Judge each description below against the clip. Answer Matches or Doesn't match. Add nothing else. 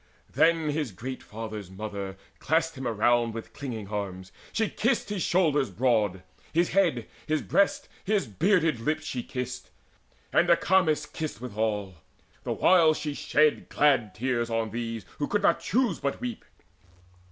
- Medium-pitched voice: Doesn't match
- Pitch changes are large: Matches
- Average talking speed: Matches